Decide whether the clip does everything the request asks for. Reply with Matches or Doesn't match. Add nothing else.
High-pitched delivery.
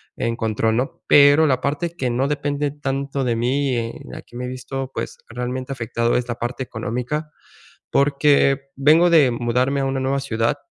Doesn't match